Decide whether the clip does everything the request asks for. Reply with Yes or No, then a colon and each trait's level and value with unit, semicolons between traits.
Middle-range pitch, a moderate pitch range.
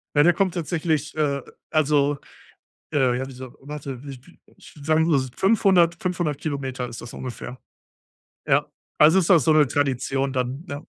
Yes: medium, 145 Hz; average, 3.4 semitones